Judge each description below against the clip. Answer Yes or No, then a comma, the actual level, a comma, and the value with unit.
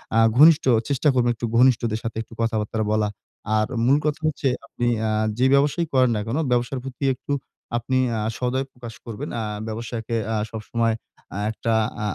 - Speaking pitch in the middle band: No, low, 120 Hz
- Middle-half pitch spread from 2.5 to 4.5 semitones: Yes, average, 2.8 semitones